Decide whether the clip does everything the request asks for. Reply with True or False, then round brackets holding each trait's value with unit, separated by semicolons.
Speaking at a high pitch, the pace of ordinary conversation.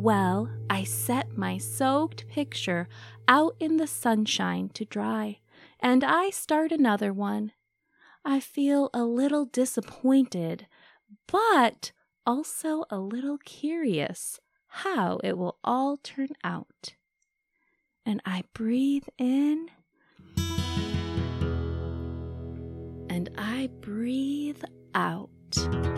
False (230 Hz; 95 wpm)